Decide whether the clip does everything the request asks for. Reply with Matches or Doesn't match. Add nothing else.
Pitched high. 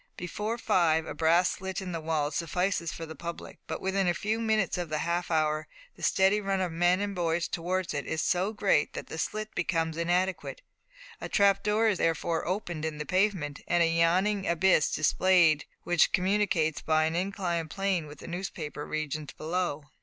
Doesn't match